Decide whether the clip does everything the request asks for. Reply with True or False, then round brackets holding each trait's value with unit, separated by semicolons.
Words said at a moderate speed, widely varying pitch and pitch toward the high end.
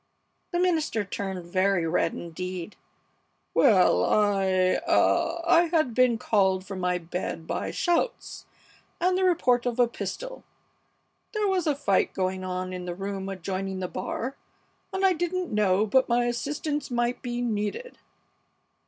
True (145 wpm; 8.3 semitones; 215 Hz)